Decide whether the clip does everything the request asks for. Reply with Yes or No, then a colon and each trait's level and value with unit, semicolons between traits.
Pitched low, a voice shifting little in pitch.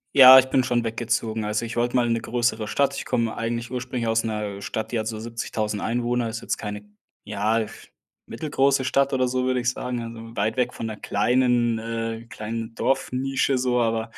Yes: low, 115 Hz; narrow, 2.0 semitones